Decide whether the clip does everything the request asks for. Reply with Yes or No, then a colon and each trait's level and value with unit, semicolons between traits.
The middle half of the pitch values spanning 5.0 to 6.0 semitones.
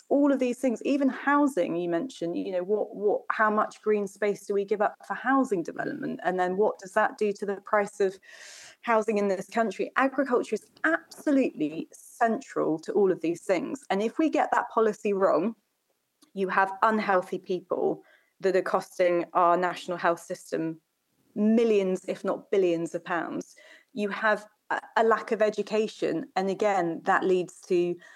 No: average, 3.8 semitones